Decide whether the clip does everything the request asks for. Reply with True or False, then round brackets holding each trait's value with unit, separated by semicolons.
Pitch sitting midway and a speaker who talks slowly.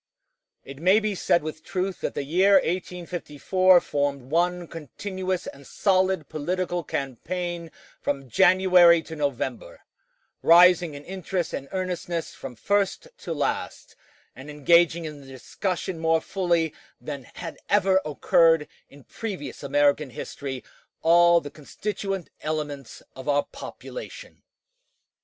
True (170 Hz; 125 wpm)